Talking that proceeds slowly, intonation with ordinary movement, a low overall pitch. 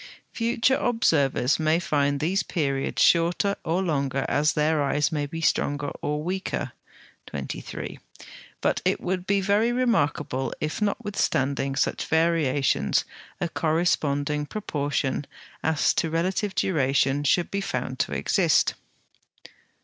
No: slow, 120 wpm; average, 4.6 semitones; medium, 155 Hz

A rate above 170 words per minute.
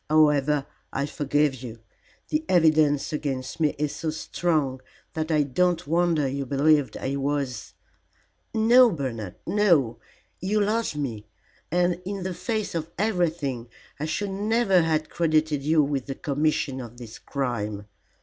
No: average, 145 wpm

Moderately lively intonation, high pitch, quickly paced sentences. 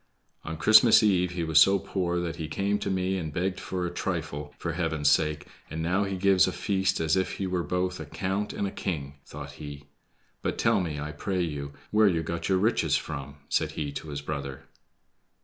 No: average, 4.1 semitones; very low, 85 Hz; fast, 215 wpm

